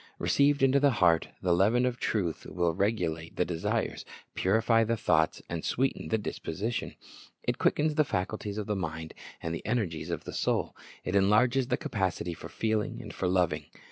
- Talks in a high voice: No, low, 100 Hz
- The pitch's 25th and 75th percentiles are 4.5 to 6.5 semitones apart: Yes, wide, 5.5 semitones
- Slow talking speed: No, average, 170 wpm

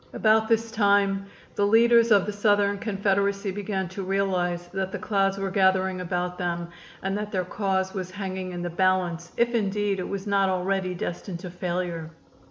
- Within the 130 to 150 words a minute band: No, average, 180 wpm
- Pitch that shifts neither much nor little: No, narrow, 1.8 semitones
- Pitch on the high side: Yes, high, 195 Hz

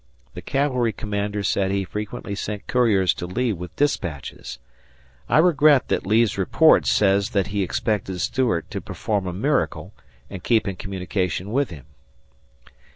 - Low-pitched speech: Yes, low, 100 Hz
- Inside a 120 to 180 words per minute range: Yes, average, 150 wpm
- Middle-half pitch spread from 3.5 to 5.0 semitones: Yes, average, 4.1 semitones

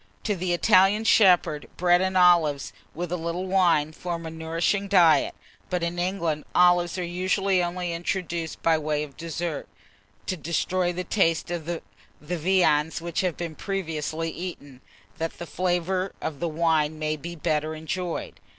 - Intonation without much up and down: Yes, narrow, 2.3 semitones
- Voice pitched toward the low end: No, medium, 170 Hz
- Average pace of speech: Yes, average, 160 wpm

